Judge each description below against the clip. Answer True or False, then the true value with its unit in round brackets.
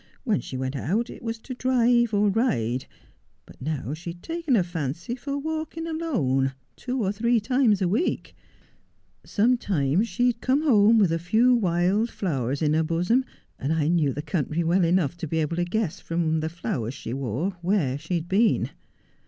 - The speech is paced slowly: False (185 wpm)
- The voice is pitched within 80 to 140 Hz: False (180 Hz)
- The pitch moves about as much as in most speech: False (7.2 semitones)